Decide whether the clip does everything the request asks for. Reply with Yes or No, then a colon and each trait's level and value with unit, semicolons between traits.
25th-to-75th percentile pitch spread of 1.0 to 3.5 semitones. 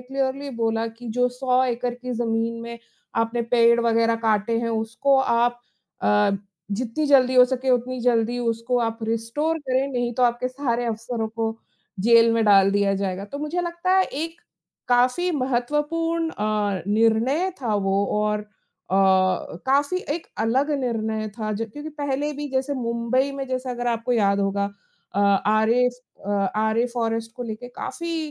Yes: average, 2.8 semitones